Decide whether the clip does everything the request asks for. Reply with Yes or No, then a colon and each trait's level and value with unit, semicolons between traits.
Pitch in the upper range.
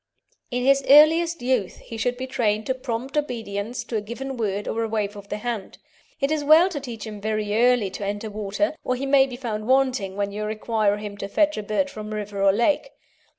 Yes: high, 230 Hz